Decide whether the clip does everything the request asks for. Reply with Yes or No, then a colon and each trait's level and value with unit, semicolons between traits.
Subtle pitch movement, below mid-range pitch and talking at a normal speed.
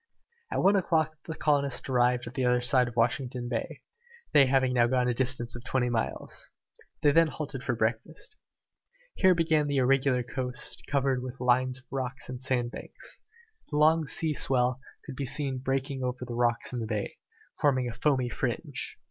Yes: narrow, 2.3 semitones; low, 130 Hz; average, 180 wpm